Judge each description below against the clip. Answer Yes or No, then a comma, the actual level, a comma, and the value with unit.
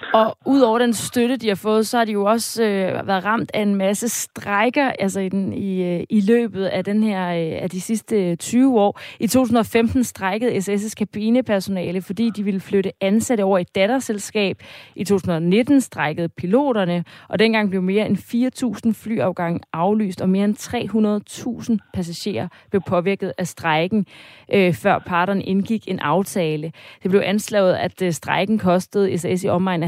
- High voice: Yes, high, 200 Hz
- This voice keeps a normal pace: Yes, average, 165 wpm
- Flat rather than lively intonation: No, average, 3.2 semitones